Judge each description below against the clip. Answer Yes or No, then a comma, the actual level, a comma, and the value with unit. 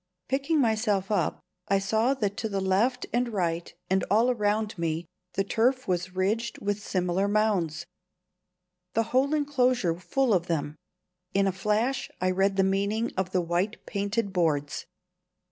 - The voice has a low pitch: No, high, 200 Hz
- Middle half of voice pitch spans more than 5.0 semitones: No, average, 3.7 semitones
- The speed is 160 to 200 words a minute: No, average, 150 wpm